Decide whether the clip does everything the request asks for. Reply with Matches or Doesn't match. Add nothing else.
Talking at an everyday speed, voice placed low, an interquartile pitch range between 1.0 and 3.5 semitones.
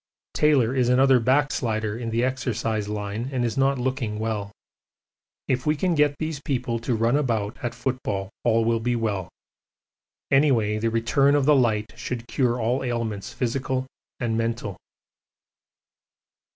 Matches